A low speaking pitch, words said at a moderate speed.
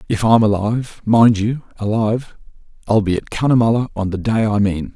Yes: low, 110 Hz; average, 160 wpm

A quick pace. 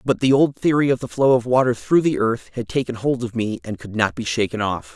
Yes: fast, 280 wpm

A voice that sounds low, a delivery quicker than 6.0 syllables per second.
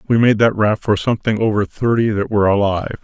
Yes: low, 110 Hz; 6.4 syllables/s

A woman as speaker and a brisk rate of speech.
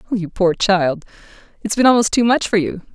No: female; average, 185 wpm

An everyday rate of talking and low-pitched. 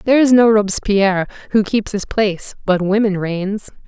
No: average, 170 wpm; high, 205 Hz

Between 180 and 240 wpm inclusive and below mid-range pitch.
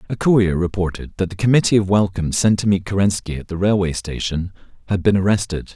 Yes: average, 200 wpm; very low, 95 Hz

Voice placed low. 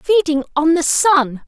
No: very high, 320 Hz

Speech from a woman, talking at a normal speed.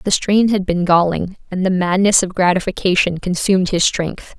Yes: female; average, 180 wpm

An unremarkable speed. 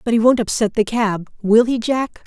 No: fast, 240 wpm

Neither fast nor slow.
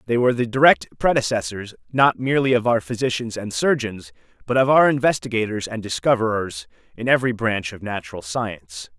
Yes: average, 160 wpm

